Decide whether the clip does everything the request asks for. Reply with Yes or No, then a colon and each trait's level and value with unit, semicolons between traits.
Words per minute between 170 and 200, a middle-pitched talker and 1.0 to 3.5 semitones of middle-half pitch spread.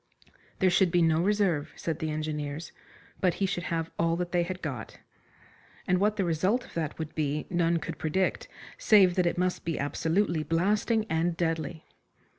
Yes: average, 180 wpm; medium, 170 Hz; narrow, 2.6 semitones